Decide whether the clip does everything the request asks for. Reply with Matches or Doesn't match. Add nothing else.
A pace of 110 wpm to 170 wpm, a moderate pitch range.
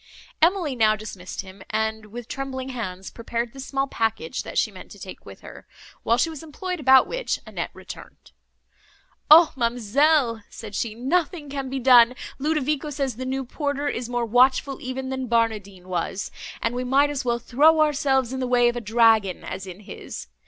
Doesn't match